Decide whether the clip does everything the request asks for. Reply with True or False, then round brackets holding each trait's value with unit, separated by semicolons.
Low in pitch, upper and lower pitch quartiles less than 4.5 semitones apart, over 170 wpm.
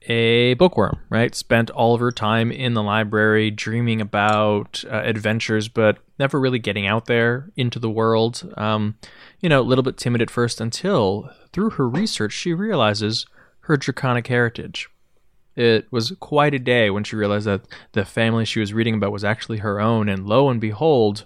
True (115 Hz; 2.7 semitones; 185 wpm)